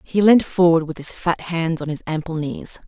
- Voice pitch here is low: No, medium, 165 Hz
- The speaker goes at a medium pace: No, fast, 230 wpm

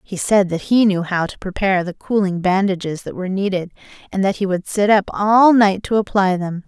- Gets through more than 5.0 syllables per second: Yes, 5.4 syllables/s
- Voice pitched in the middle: No, high, 195 Hz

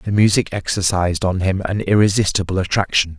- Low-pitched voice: Yes, very low, 95 Hz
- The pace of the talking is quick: No, average, 150 wpm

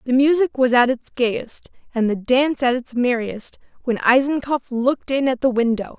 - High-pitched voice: Yes, very high, 250 Hz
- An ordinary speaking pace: Yes, average, 190 wpm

